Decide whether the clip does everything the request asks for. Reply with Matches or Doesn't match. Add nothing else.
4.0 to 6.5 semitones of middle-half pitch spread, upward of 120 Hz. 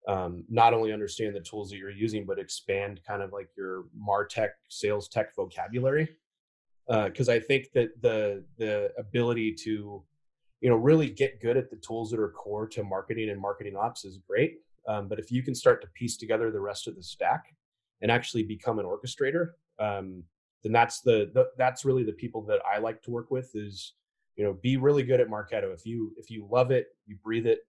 Doesn't match